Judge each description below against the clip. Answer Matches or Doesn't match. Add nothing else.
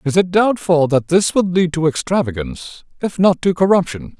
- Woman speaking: Doesn't match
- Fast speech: Doesn't match